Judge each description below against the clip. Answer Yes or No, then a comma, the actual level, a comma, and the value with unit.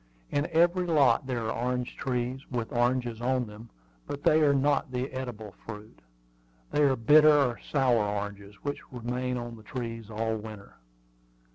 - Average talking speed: Yes, average, 160 wpm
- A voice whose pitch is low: Yes, low, 125 Hz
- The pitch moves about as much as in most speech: Yes, average, 3.3 semitones